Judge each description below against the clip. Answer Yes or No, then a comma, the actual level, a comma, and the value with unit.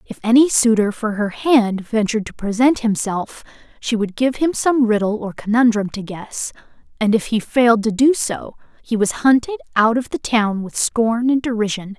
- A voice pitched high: Yes, high, 230 Hz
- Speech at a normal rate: Yes, average, 190 wpm